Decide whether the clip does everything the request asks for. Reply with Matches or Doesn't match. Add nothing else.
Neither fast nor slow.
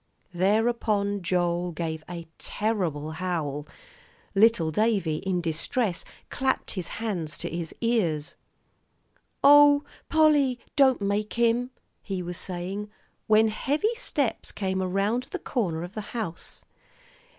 Doesn't match